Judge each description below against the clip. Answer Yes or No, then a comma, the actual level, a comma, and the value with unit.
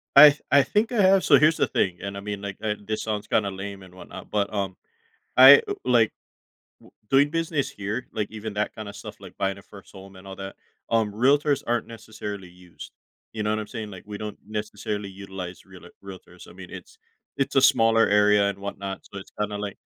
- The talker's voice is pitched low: Yes, low, 105 Hz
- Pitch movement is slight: No, average, 3.3 semitones